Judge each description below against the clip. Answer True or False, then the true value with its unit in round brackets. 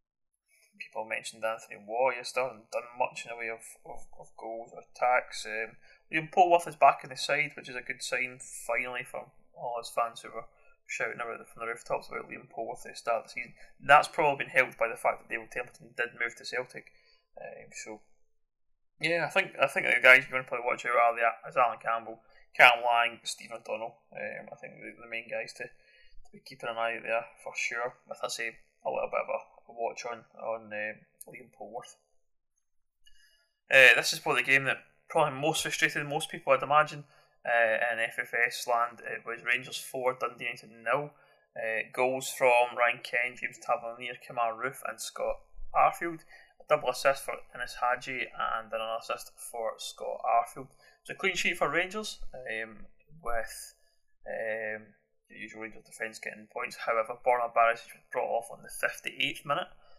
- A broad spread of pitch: False (4.4 semitones)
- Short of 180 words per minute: False (195 wpm)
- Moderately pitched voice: False (120 Hz)